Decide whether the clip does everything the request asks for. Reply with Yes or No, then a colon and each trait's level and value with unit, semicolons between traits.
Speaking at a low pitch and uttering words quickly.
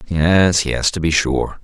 No: very low, 85 Hz; average, 185 wpm